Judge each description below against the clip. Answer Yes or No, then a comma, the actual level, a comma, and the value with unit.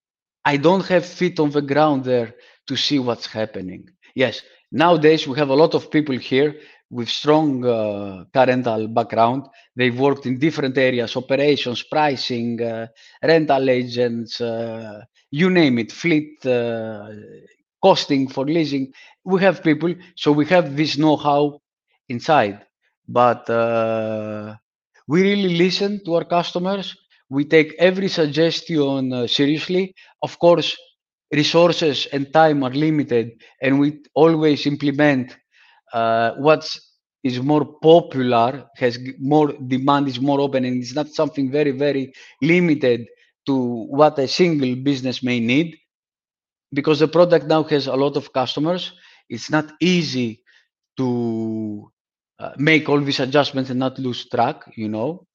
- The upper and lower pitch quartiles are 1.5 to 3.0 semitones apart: No, average, 4.1 semitones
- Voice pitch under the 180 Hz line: Yes, medium, 140 Hz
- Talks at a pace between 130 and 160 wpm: Yes, average, 140 wpm